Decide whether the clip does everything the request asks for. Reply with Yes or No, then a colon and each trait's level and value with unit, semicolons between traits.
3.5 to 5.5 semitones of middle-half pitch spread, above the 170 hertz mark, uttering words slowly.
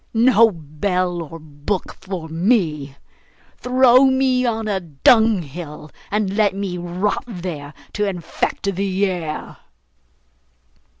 Yes: average, 4.9 semitones; high, 190 Hz; slow, 110 wpm